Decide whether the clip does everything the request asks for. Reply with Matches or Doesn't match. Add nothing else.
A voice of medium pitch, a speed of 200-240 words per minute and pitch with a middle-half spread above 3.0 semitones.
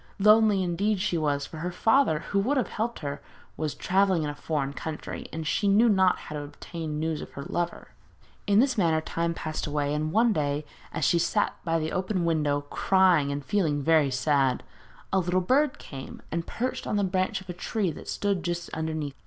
Matches